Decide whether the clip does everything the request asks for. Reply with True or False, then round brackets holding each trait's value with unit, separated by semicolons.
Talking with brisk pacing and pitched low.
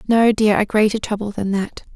False (215 wpm; 210 Hz)